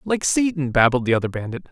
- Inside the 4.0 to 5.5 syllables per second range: No, 6.2 syllables/s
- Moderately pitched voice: Yes, medium, 145 Hz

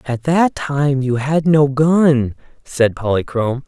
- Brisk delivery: No, average, 145 wpm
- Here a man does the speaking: Yes, male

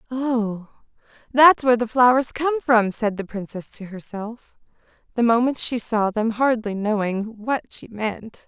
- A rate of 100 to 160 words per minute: Yes, average, 155 wpm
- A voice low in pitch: No, high, 230 Hz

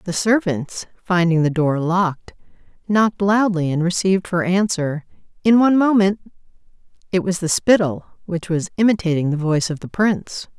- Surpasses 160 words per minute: No, average, 155 wpm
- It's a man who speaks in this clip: No, female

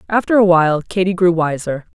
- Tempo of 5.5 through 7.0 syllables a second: Yes, 6.0 syllables/s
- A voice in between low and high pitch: Yes, medium, 175 Hz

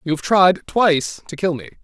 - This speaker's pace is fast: Yes, fast, 230 wpm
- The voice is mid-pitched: Yes, medium, 160 Hz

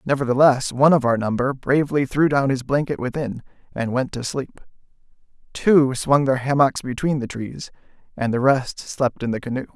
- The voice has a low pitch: Yes, low, 130 Hz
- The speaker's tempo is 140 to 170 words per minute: No, average, 180 wpm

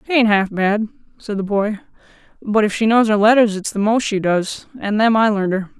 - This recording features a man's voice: No, female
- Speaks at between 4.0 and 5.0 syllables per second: No, 5.5 syllables/s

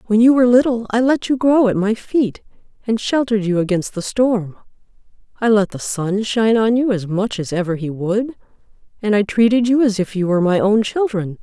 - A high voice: Yes, high, 215 Hz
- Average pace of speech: No, fast, 215 wpm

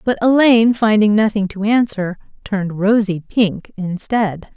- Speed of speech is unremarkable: No, slow, 130 wpm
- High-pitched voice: Yes, high, 210 Hz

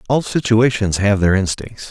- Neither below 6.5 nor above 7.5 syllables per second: No, 4.7 syllables/s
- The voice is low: Yes, low, 105 Hz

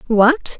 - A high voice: Yes, very high, 255 Hz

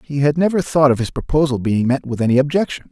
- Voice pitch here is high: No, medium, 140 Hz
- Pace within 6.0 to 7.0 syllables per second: Yes, 6.4 syllables/s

